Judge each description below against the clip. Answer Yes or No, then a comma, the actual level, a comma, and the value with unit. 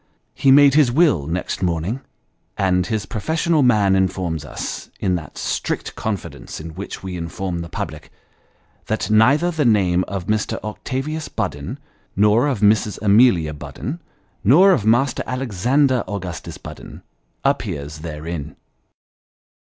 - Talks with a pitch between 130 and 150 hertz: No, low, 105 Hz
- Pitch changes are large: Yes, wide, 6.7 semitones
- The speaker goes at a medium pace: No, slow, 130 wpm